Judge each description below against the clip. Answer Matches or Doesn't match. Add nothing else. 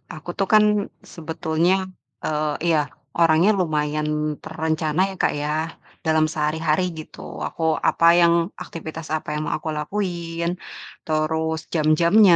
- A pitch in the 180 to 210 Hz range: Doesn't match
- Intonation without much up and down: Matches